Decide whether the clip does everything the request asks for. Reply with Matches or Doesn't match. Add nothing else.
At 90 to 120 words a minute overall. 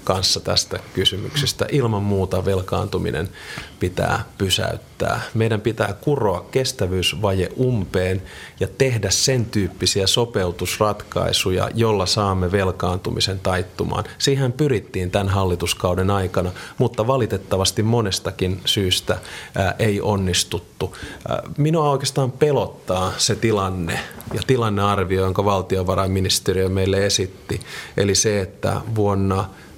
Matches